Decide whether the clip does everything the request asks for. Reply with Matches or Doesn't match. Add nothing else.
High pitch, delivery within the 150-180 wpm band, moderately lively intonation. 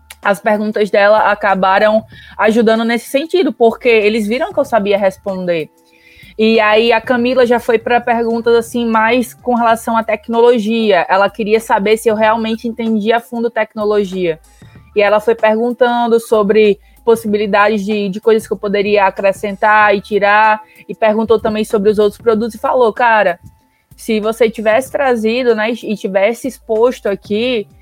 Doesn't match